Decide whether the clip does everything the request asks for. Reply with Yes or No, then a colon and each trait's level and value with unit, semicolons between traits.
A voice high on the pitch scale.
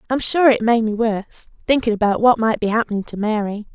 Yes: high, 225 Hz